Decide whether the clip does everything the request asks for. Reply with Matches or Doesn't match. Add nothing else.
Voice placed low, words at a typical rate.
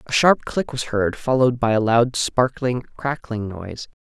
Matches